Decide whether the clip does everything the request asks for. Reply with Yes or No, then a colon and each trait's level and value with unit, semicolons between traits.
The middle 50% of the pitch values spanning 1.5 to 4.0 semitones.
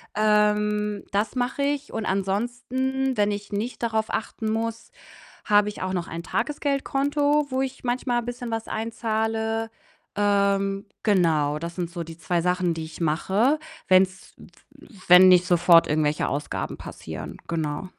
No: average, 4.9 semitones